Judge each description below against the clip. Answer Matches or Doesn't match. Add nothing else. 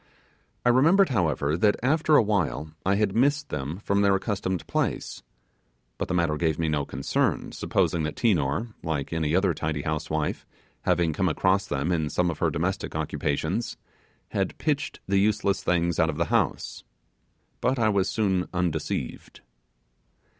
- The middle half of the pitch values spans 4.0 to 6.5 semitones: Matches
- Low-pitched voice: Matches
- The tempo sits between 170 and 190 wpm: Doesn't match